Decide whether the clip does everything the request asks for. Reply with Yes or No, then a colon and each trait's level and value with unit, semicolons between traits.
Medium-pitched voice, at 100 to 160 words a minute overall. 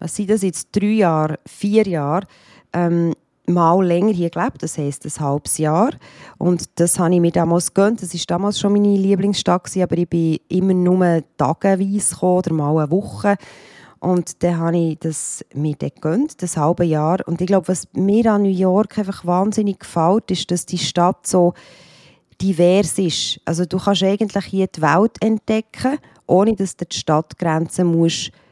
No: medium, 180 Hz; average, 175 wpm